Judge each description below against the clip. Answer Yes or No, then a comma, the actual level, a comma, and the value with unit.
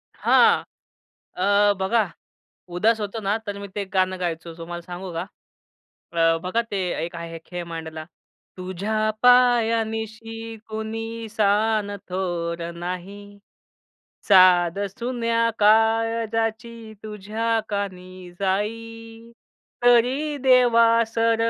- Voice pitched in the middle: No, high, 210 Hz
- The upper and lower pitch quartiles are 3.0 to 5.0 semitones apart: Yes, average, 3.7 semitones